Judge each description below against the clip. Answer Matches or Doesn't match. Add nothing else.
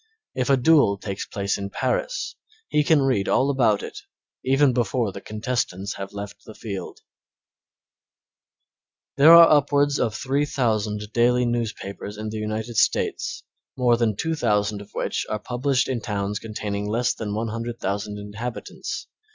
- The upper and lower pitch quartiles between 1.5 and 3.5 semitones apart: Doesn't match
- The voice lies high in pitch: Doesn't match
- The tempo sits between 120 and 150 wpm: Matches